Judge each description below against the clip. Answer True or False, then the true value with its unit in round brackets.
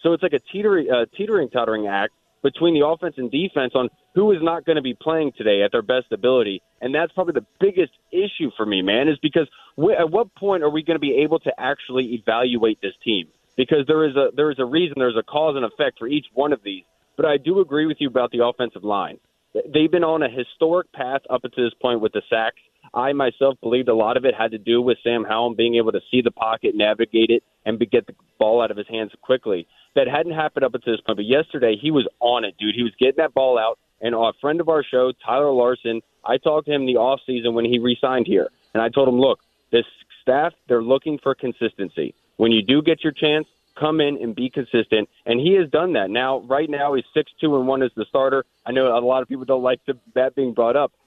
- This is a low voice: True (130 Hz)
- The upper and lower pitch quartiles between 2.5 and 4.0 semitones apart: False (4.6 semitones)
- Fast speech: True (250 wpm)